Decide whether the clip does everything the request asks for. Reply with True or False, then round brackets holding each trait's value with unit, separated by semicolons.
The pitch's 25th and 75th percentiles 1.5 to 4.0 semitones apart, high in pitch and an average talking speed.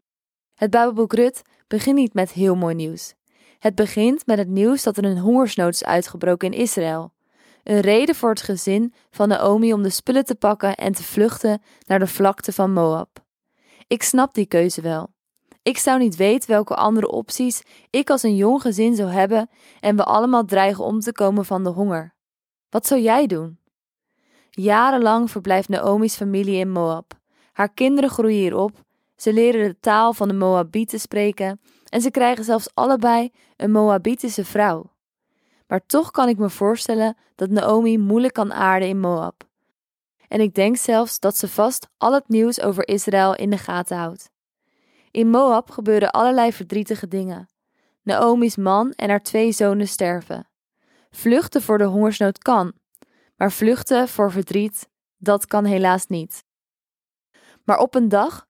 True (3.2 semitones; 210 Hz; 165 wpm)